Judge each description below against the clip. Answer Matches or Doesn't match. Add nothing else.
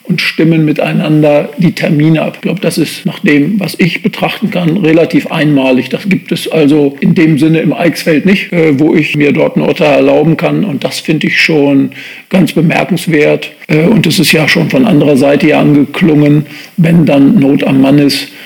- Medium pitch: Matches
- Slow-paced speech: Doesn't match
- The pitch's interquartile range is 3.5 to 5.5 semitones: Doesn't match